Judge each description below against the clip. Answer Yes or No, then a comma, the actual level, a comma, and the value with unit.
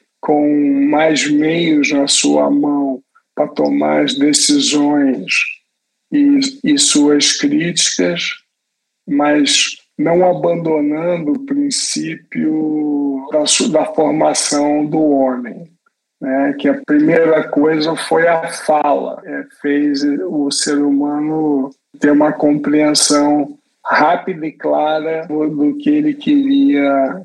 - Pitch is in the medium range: Yes, medium, 150 Hz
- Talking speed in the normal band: No, slow, 105 wpm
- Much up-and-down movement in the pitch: No, average, 3.1 semitones